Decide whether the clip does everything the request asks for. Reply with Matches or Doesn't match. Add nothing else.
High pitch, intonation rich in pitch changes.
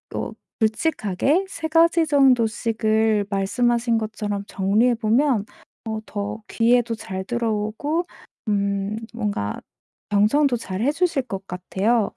Doesn't match